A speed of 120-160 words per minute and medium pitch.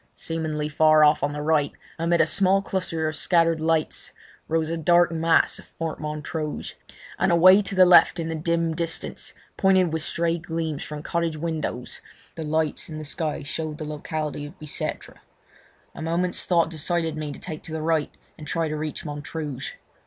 No: average, 180 wpm; medium, 160 Hz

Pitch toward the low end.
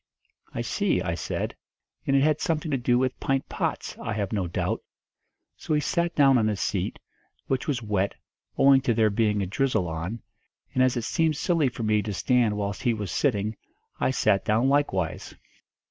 Yes: low, 120 Hz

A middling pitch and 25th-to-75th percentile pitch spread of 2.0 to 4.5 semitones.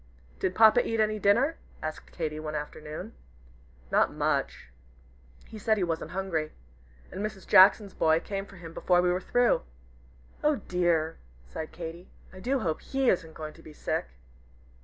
No: medium, 180 Hz; average, 5.0 semitones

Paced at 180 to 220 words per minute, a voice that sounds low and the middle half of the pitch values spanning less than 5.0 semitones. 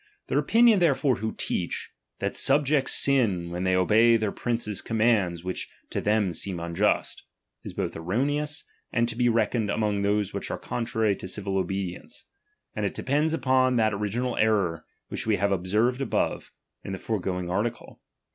No: average, 165 wpm; low, 110 Hz; average, 4.5 semitones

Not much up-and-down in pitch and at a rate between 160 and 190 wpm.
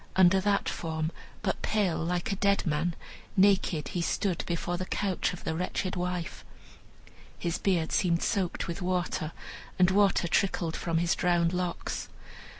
No: narrow, 2.0 semitones; average, 150 wpm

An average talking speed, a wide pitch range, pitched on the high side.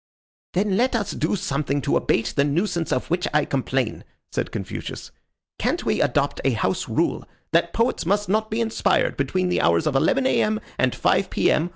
No: average, 185 wpm; wide, 7.1 semitones; medium, 175 Hz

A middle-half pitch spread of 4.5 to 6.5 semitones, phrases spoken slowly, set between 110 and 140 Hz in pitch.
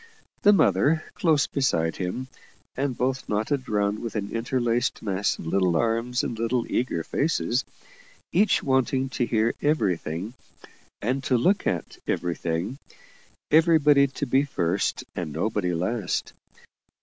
Yes: average, 5.3 semitones; slow, 130 wpm; low, 120 Hz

